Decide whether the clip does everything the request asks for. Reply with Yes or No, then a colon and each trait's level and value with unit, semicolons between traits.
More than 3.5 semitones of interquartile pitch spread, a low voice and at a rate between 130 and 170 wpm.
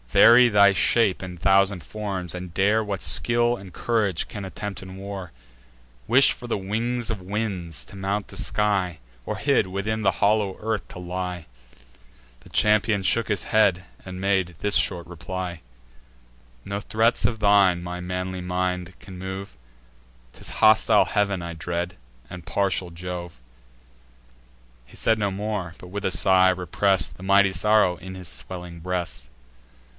No: narrow, 2.5 semitones; very low, 95 Hz; average, 155 wpm